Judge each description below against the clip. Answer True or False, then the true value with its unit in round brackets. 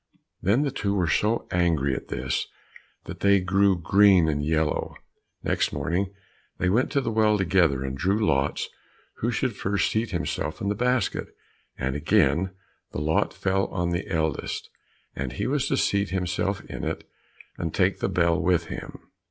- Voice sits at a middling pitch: False (90 Hz)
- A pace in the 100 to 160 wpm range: False (170 wpm)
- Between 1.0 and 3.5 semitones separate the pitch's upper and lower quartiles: False (4.0 semitones)